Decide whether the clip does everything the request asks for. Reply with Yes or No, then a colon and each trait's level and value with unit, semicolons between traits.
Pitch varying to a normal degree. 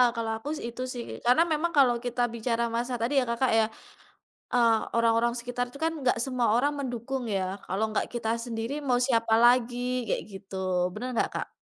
No: narrow, 1.7 semitones